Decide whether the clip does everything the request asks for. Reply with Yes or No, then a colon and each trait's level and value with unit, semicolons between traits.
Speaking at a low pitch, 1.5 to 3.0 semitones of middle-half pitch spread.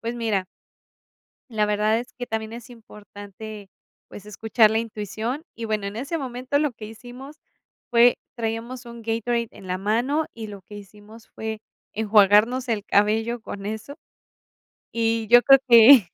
No: high, 225 Hz; narrow, 2.4 semitones